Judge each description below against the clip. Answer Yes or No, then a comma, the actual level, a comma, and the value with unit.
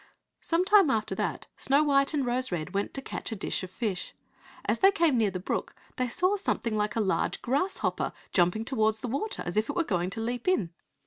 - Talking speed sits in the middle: No, fast, 220 wpm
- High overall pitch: Yes, high, 240 Hz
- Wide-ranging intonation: Yes, wide, 6.0 semitones